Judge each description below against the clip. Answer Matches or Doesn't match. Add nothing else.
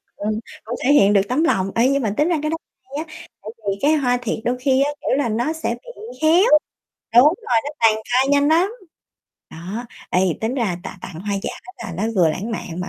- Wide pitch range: Matches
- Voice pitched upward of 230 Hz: Matches